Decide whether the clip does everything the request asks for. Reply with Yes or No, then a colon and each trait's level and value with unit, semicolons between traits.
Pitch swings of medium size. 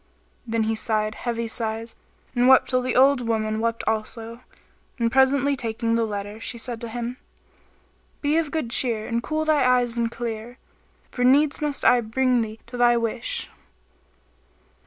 No: narrow, 2.2 semitones